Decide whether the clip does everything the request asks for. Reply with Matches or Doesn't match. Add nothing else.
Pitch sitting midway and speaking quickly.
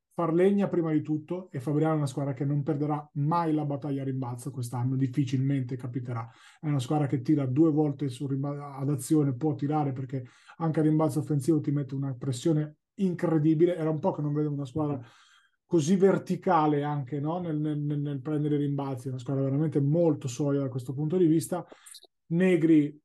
Matches